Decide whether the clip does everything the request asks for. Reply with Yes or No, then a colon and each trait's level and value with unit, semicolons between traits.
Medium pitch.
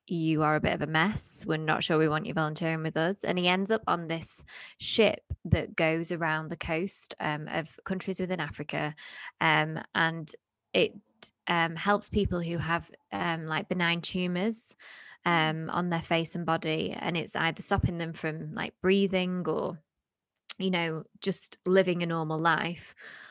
Yes: medium, 165 Hz